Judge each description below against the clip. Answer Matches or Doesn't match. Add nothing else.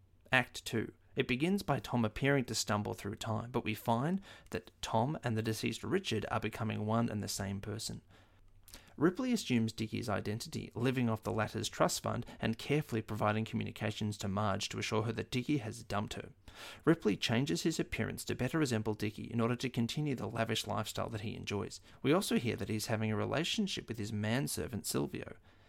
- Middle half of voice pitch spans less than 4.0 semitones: Matches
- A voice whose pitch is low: Matches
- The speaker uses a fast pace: Doesn't match